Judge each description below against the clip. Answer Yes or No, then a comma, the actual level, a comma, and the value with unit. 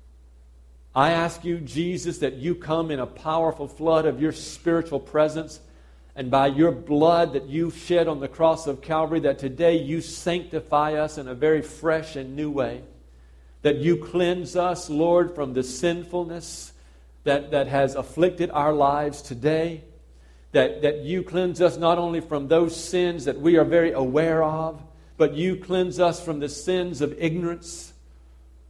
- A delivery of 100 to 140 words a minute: No, average, 165 wpm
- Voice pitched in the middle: Yes, medium, 155 Hz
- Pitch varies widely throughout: No, average, 3.6 semitones